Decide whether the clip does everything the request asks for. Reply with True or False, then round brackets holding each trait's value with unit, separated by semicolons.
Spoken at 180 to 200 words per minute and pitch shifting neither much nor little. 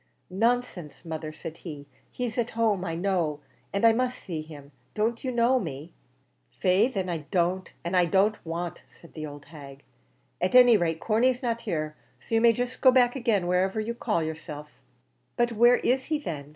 False (190 wpm; 6.5 semitones)